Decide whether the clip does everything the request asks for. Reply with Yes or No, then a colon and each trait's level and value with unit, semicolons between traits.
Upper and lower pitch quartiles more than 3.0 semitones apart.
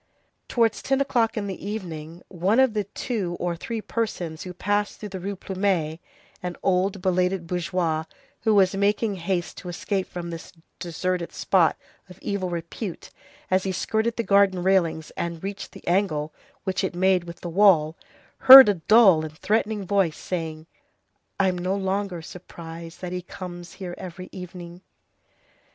No: average, 2.7 semitones